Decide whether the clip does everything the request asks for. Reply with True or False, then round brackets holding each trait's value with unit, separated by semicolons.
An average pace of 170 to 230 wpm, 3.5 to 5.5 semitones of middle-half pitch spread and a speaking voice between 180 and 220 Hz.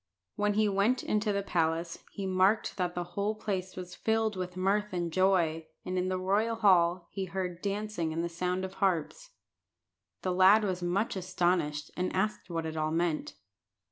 False (180 wpm; 2.6 semitones; 185 Hz)